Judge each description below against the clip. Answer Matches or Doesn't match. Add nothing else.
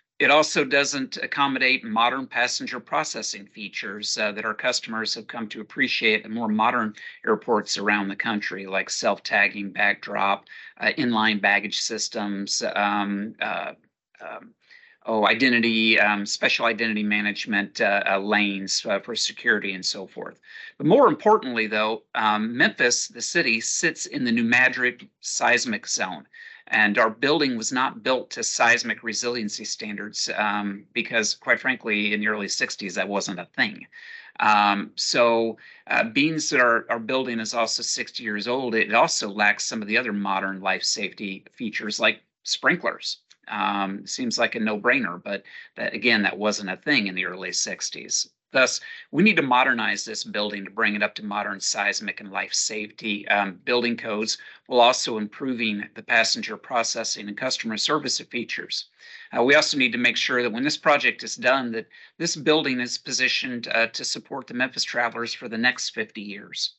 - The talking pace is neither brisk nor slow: Matches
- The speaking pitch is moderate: Doesn't match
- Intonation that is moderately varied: Matches